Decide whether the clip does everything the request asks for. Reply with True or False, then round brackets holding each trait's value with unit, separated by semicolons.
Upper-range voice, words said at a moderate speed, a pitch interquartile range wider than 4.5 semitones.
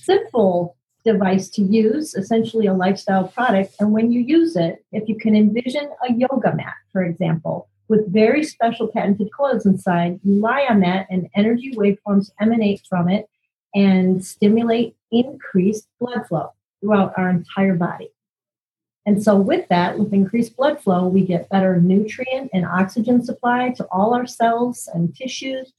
False (210 Hz; 160 wpm; 4.0 semitones)